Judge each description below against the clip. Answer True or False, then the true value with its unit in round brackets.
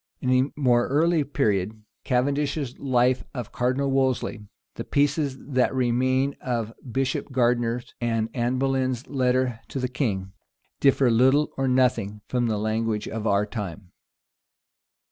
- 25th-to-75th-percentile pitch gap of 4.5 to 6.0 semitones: False (2.8 semitones)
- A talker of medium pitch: False (125 Hz)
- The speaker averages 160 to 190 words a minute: False (135 wpm)